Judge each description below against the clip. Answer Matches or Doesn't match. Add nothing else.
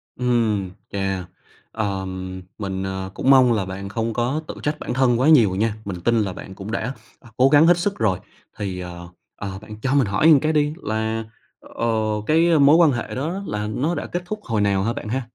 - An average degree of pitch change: Doesn't match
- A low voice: Matches